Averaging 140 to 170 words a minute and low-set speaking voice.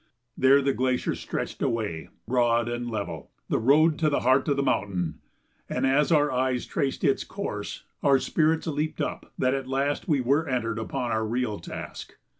No: average, 180 wpm; low, 130 Hz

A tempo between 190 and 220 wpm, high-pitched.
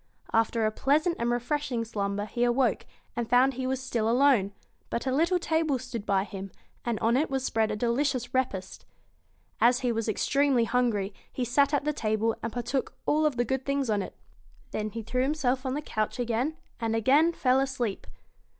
Yes: average, 195 wpm; high, 245 Hz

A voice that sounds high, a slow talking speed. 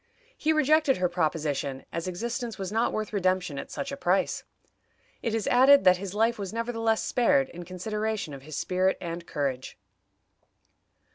No: high, 195 Hz; average, 160 wpm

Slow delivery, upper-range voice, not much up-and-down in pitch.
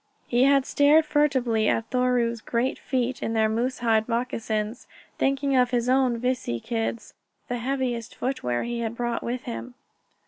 No: average, 160 wpm; high, 240 Hz; narrow, 2.3 semitones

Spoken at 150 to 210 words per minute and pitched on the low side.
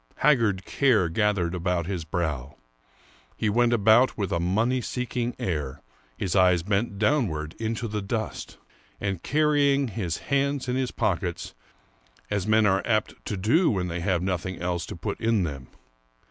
Yes: average, 160 wpm; low, 100 Hz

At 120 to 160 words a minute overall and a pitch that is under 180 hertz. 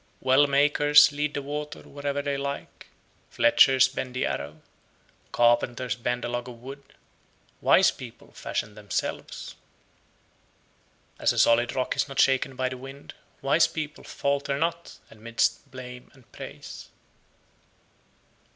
Yes: slow, 135 wpm; low, 135 Hz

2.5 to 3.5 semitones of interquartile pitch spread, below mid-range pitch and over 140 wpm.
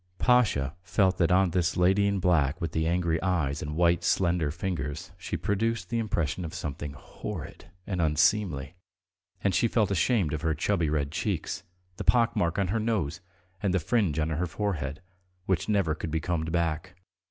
No: average, 3.9 semitones; very low, 85 Hz; average, 180 wpm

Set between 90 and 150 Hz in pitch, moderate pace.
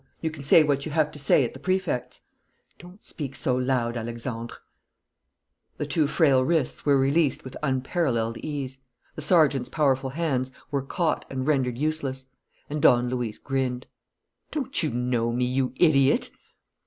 Yes: low, 135 Hz; average, 155 wpm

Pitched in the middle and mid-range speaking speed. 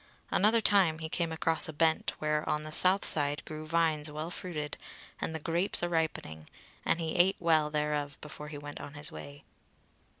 Yes: medium, 155 Hz; average, 190 wpm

